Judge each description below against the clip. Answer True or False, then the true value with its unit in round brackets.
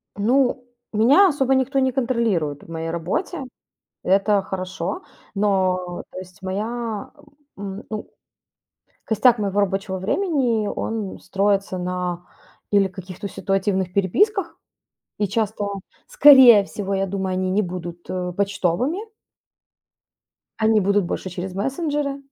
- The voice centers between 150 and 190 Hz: False (200 Hz)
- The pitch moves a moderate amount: True (4.4 semitones)